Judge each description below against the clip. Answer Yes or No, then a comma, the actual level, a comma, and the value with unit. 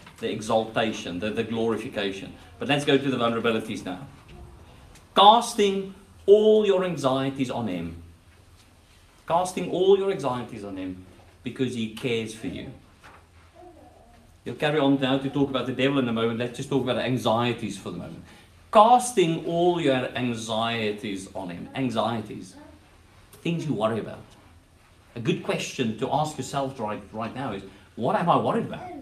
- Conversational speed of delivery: Yes, average, 155 wpm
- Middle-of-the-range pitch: No, low, 115 Hz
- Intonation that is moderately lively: No, wide, 5.7 semitones